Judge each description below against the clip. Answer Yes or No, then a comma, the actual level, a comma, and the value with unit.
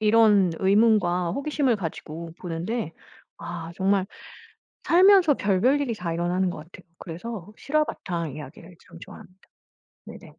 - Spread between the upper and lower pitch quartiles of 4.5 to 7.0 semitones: Yes, average, 5.1 semitones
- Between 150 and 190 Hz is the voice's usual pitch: Yes, medium, 185 Hz